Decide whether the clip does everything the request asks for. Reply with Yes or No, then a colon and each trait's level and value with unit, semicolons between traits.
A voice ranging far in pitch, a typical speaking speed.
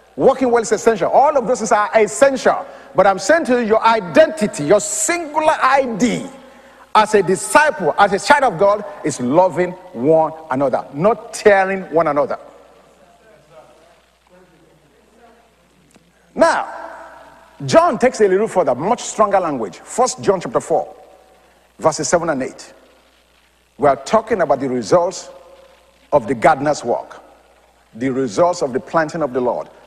Yes: wide, 6.4 semitones; average, 145 wpm